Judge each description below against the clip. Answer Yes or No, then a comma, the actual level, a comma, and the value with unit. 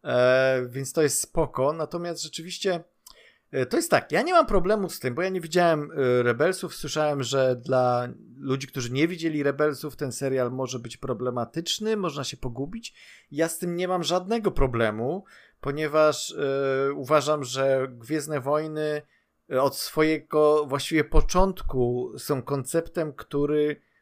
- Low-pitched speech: No, medium, 150 Hz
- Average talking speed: Yes, average, 140 wpm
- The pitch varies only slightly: No, average, 3.7 semitones